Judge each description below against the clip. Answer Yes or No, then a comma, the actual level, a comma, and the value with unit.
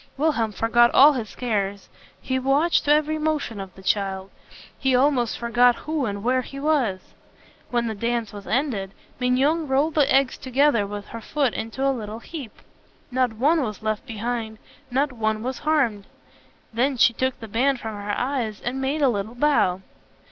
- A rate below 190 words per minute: Yes, average, 175 wpm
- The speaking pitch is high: Yes, high, 245 Hz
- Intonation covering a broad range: No, average, 4.1 semitones